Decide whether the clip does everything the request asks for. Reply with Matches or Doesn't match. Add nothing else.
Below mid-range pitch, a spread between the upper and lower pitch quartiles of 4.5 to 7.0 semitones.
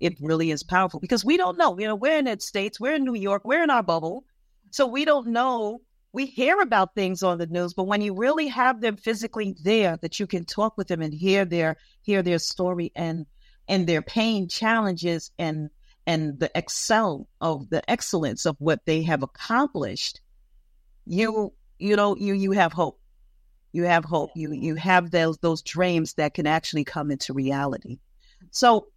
Doesn't match